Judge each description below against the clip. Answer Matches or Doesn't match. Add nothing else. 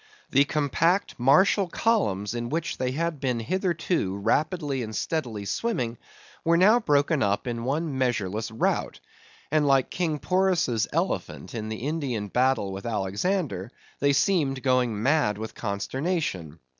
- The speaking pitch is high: Doesn't match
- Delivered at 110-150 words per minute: Matches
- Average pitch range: Doesn't match